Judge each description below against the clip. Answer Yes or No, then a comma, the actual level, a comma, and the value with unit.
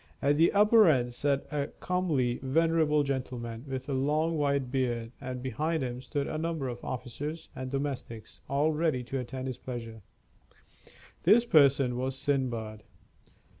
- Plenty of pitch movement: No, average, 3.4 semitones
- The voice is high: No, low, 135 Hz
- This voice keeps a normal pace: Yes, average, 150 wpm